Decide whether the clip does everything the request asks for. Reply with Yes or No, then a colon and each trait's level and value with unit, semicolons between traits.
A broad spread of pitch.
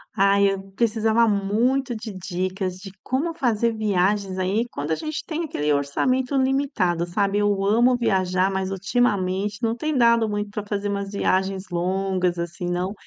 No: average, 3.8 semitones